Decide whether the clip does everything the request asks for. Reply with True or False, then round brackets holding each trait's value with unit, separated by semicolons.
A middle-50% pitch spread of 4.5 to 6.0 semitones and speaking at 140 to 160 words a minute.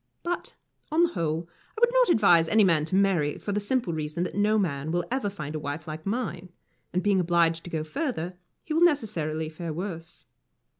False (5.1 semitones; 205 wpm)